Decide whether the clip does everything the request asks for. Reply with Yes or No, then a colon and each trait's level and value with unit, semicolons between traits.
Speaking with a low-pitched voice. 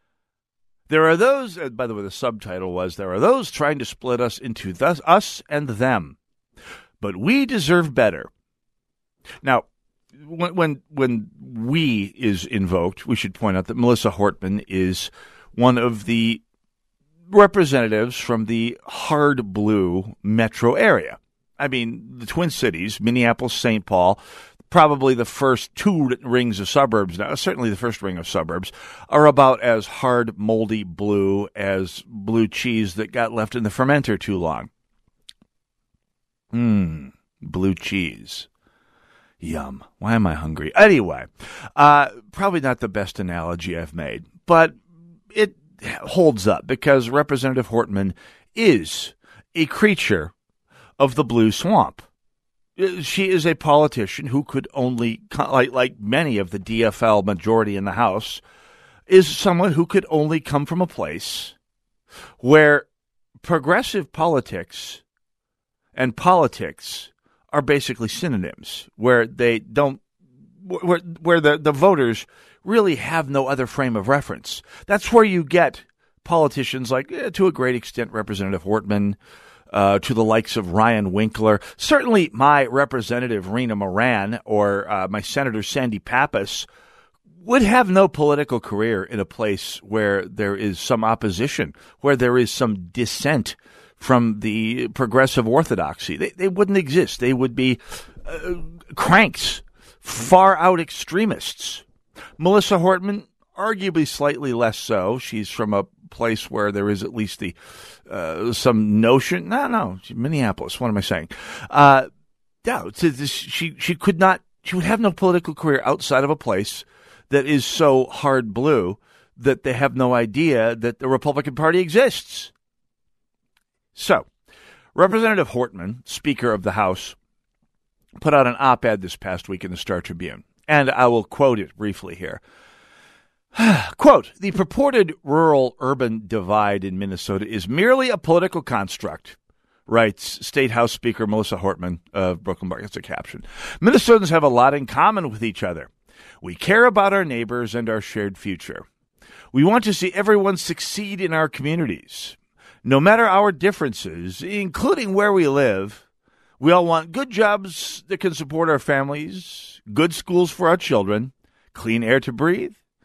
Yes: low, 130 Hz